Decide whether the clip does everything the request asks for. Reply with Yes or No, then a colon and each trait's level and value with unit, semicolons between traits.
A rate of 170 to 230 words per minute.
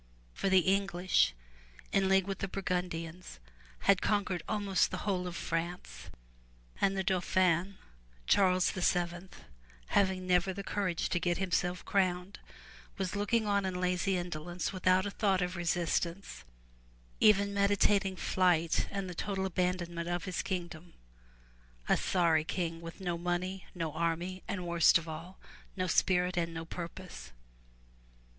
No: average, 145 wpm